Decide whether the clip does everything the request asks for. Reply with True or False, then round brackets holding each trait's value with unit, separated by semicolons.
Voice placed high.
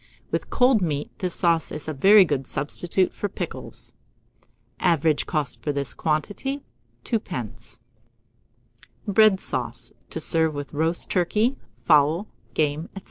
False (165 Hz)